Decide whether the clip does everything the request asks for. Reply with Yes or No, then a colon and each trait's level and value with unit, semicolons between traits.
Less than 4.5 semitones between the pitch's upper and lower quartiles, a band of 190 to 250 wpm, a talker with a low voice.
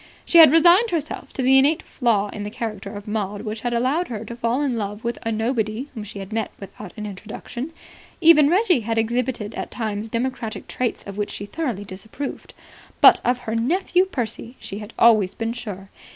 No: average, 4.0 semitones; average, 200 wpm; high, 230 Hz